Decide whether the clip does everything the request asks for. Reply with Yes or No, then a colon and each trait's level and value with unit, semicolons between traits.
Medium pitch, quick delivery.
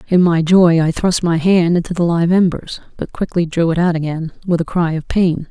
Yes: medium, 170 Hz; fast, 240 wpm